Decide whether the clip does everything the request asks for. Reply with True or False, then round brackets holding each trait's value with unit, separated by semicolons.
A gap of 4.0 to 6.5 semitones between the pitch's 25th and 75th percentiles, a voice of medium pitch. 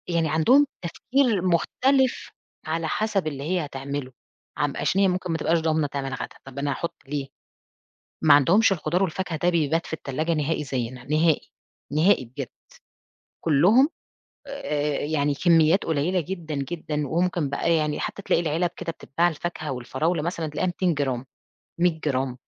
False (3.5 semitones; 160 Hz)